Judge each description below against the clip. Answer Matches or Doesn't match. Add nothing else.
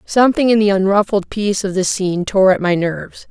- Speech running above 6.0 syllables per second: Doesn't match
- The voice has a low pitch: Doesn't match